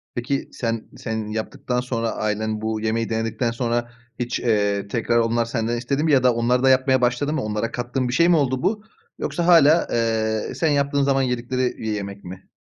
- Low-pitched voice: Yes, low, 120 Hz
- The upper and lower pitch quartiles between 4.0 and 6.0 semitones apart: No, average, 2.9 semitones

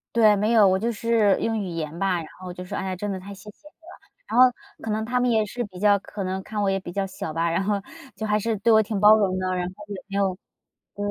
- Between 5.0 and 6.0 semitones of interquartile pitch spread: No, average, 2.7 semitones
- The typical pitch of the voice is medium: No, high, 200 Hz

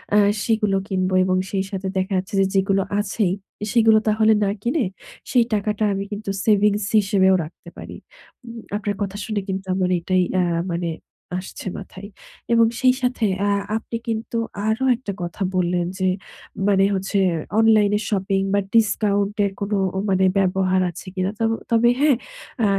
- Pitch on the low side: No, high, 200 Hz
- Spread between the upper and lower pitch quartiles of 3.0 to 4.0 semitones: No, narrow, 2.5 semitones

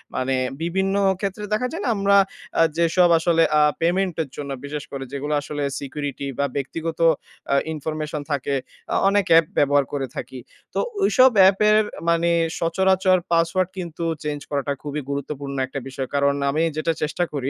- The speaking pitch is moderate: Yes, medium, 155 Hz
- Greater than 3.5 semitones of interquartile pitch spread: Yes, average, 4.4 semitones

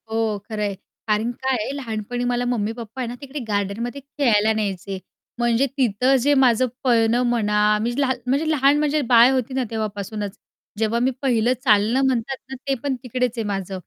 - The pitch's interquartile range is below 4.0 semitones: Yes, average, 3.4 semitones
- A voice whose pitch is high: Yes, high, 235 Hz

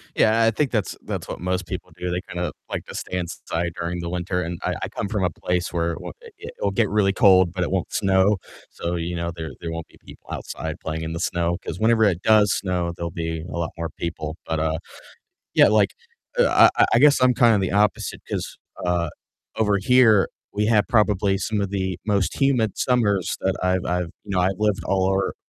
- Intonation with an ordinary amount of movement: Yes, average, 3.4 semitones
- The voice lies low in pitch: Yes, very low, 95 Hz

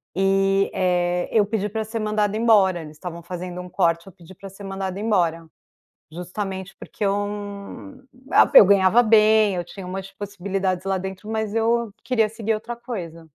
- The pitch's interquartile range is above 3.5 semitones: No, average, 2.9 semitones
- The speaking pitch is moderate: No, high, 195 Hz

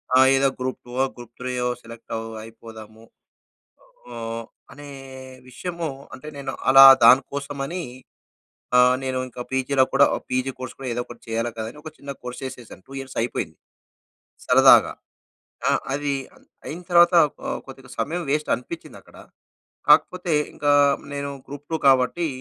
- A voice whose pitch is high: No, low, 135 Hz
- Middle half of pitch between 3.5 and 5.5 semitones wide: No, average, 2.9 semitones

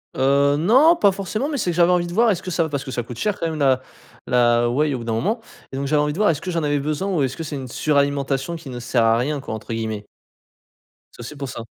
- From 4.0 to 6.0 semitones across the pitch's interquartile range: Yes, average, 5.1 semitones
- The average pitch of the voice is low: No, medium, 145 Hz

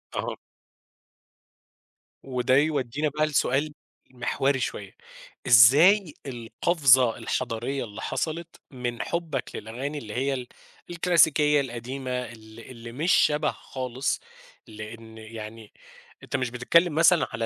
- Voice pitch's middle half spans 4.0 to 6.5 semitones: Yes, average, 4.4 semitones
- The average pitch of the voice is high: No, low, 130 Hz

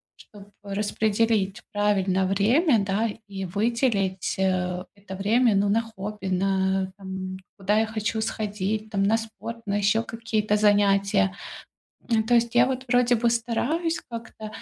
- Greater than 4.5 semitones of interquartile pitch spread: No, average, 2.7 semitones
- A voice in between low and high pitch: No, high, 210 Hz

